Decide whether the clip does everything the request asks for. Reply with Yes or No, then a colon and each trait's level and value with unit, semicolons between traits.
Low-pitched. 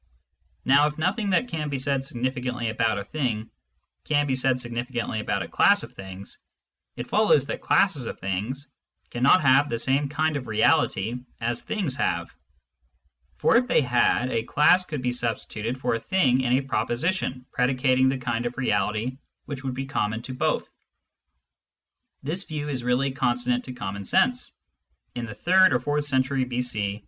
Yes: low, 130 Hz